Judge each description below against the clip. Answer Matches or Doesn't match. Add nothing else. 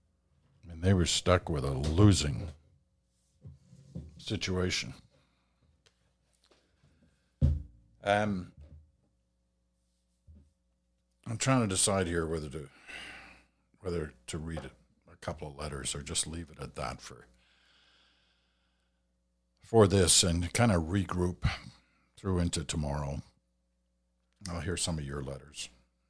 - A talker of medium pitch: Doesn't match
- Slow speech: Matches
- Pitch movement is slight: Doesn't match